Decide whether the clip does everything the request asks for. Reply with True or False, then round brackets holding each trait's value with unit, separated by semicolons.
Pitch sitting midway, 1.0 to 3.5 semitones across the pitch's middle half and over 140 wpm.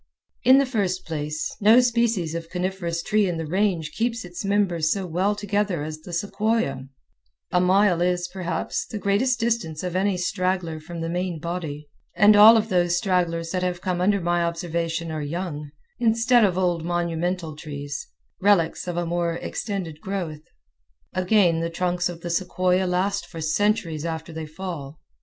True (180 Hz; 3.2 semitones; 170 wpm)